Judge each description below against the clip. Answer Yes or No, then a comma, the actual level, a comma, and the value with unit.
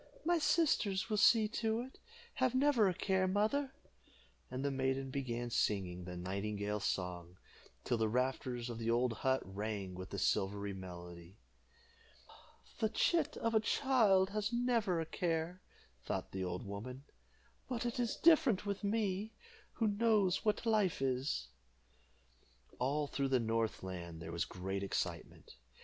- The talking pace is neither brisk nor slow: Yes, average, 150 wpm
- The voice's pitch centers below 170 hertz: Yes, low, 135 Hz